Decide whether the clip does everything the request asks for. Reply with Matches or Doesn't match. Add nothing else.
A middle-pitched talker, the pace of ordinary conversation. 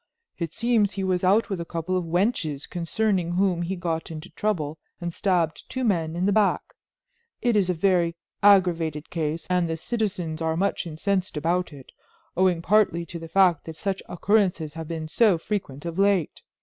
Matches